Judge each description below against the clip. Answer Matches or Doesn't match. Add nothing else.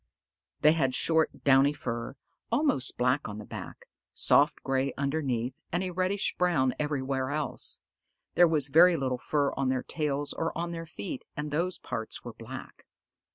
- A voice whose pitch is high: Doesn't match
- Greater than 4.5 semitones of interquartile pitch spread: Doesn't match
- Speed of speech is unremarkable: Matches